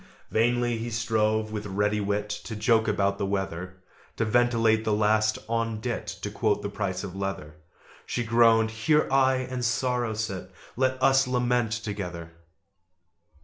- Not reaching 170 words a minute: Yes, average, 150 wpm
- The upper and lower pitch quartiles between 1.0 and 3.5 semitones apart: Yes, average, 2.7 semitones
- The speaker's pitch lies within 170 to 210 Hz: No, low, 110 Hz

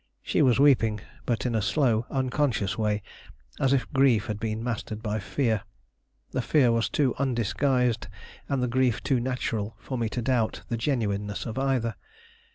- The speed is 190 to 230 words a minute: No, average, 165 wpm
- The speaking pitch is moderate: No, low, 120 Hz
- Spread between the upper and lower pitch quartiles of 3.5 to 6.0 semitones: No, average, 3.1 semitones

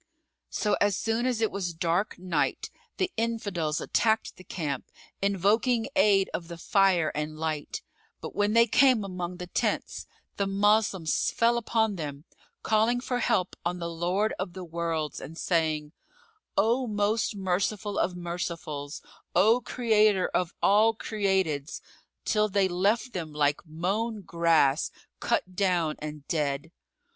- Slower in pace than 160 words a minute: Yes, average, 140 wpm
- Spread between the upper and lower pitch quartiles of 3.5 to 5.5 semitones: Yes, average, 4.5 semitones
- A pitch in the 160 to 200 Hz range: Yes, high, 190 Hz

